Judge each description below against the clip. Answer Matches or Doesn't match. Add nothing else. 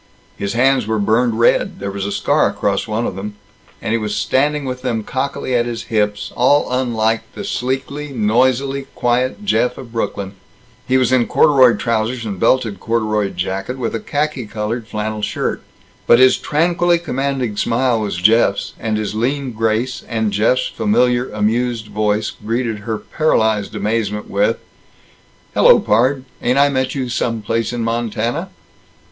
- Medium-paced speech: Matches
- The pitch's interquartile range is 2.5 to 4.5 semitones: Matches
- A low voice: Matches